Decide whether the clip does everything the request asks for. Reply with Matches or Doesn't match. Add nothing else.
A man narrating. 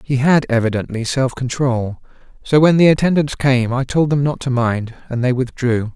Matches